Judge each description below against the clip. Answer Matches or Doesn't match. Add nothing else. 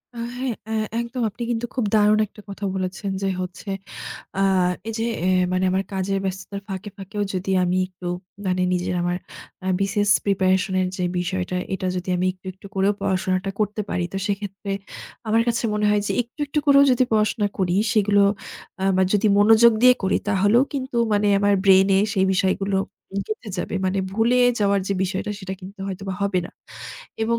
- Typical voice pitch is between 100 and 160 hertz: Doesn't match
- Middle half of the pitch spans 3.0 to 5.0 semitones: Doesn't match